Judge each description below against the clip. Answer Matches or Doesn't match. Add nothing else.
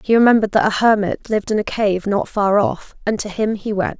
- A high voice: Matches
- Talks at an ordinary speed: Doesn't match